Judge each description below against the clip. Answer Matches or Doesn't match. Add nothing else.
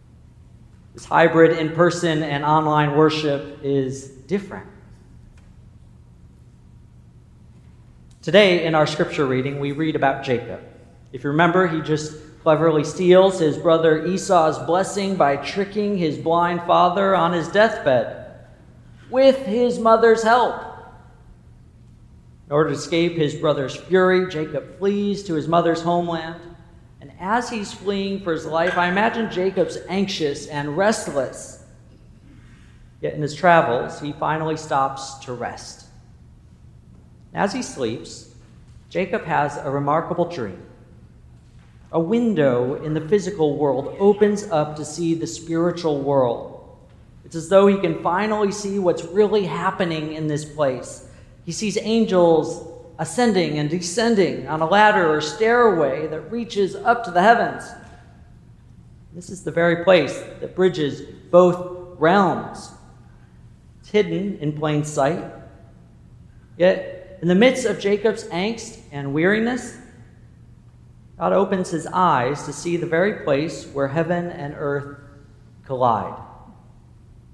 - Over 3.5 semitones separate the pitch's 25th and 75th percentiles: Matches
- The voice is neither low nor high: Matches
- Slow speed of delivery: Matches